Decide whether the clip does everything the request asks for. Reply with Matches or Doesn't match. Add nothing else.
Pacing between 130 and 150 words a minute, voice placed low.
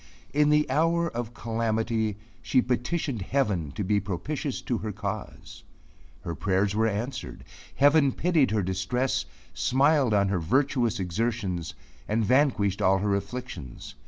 Matches